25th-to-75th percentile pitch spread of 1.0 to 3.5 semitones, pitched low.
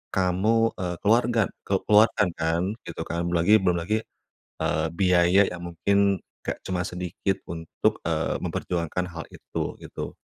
Yes: average, 2.7 semitones; very low, 90 Hz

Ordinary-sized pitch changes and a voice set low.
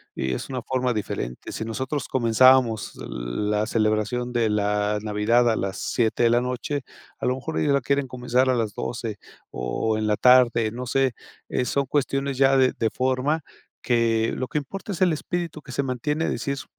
Yes: average, 3.4 semitones; low, 125 Hz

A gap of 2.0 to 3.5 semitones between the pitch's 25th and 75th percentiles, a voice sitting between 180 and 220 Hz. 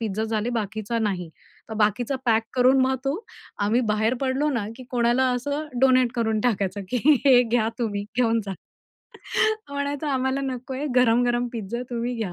No: average, 2.9 semitones; high, 240 Hz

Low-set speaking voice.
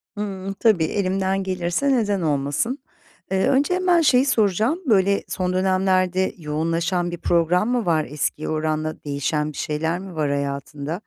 No: medium, 185 Hz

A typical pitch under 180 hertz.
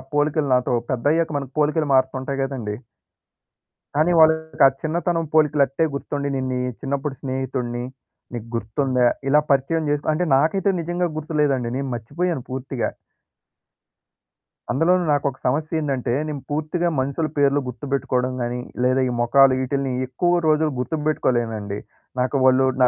Yes: medium, 140 Hz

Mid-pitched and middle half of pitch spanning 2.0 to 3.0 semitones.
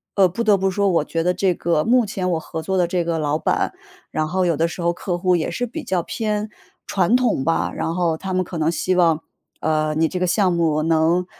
Yes: medium, 175 Hz; average, 2.7 semitones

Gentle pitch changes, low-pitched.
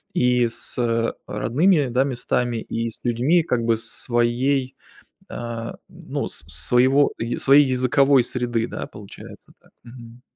Yes: narrow, 2.2 semitones; low, 120 Hz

